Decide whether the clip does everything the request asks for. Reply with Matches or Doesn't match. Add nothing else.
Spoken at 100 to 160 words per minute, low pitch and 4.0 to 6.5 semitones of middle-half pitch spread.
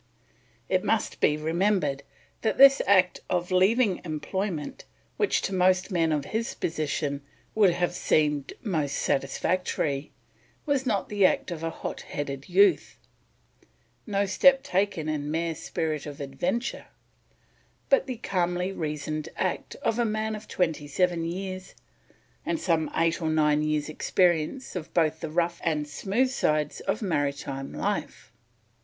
Doesn't match